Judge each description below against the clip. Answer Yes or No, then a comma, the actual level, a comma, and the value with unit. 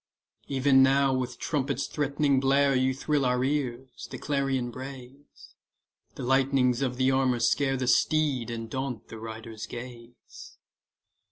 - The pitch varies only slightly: Yes, narrow, 1.9 semitones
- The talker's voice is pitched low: Yes, low, 130 Hz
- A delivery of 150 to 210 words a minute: No, average, 140 wpm